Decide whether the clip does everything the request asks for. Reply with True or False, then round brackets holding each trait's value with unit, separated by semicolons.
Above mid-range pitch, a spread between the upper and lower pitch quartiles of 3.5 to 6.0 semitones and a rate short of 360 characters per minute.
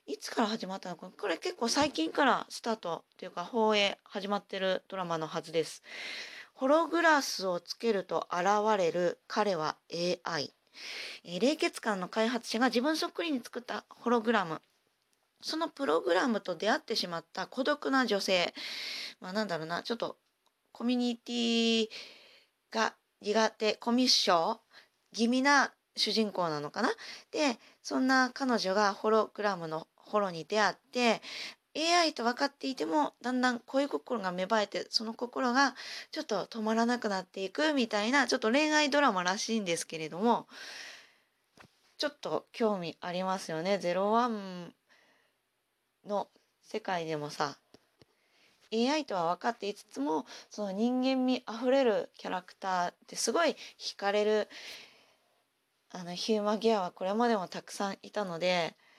True (220 Hz; 5.3 semitones; 310 characters per minute)